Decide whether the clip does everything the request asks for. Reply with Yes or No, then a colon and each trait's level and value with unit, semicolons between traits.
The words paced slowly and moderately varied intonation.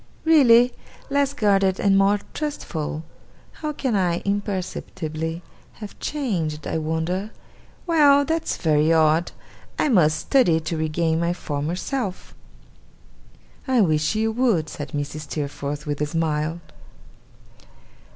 No: slow, 120 wpm; wide, 6.3 semitones